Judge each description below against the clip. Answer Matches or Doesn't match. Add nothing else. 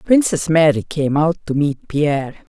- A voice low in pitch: Doesn't match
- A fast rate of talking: Doesn't match